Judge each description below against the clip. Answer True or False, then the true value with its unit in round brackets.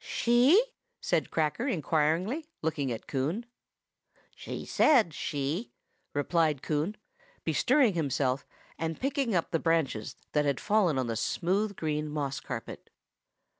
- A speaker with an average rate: False (130 wpm)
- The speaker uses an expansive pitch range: True (6.7 semitones)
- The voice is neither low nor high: True (160 Hz)